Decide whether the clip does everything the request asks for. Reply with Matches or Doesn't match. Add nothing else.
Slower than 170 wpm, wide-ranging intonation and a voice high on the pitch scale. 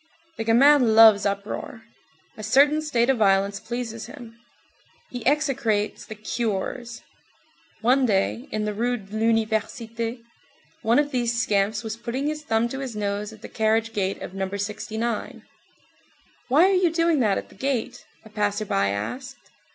Doesn't match